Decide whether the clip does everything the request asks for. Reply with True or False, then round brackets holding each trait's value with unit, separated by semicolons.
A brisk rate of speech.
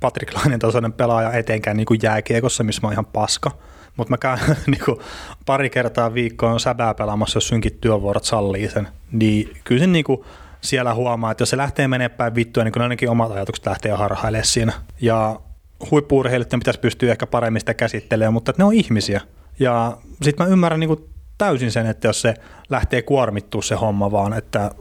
True (190 wpm)